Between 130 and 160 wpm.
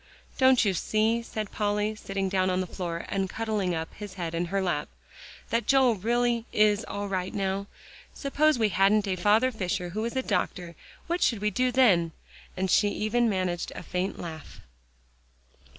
No: average, 180 wpm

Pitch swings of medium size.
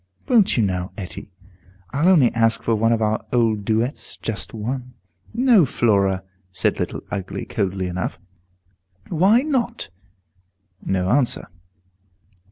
No: wide, 7.0 semitones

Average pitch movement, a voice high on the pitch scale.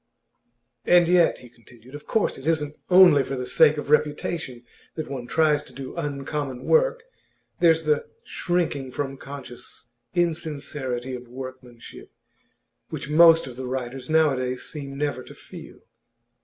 No: average, 3.8 semitones; medium, 145 Hz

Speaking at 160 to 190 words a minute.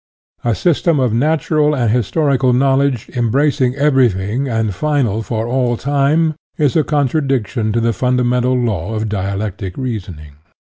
No: average, 140 wpm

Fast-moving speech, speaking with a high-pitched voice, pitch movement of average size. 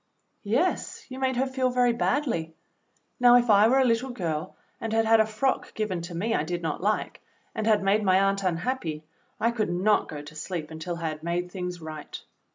No: fast, 210 wpm; high, 200 Hz; wide, 5.7 semitones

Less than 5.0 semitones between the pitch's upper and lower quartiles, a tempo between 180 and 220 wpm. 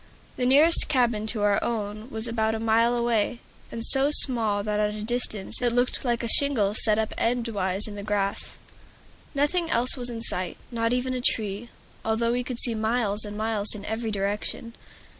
Yes: narrow, 2.5 semitones; average, 190 wpm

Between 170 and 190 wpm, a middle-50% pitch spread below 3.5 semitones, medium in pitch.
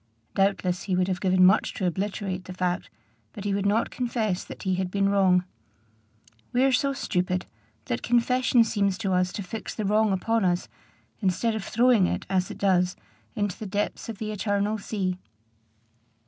No: average, 180 wpm; average, 3.0 semitones; high, 195 Hz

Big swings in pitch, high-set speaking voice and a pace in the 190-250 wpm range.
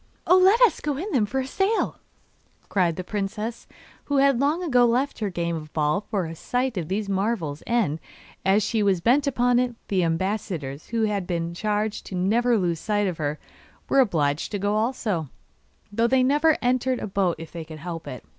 Yes: wide, 6.4 semitones; high, 210 Hz; average, 200 wpm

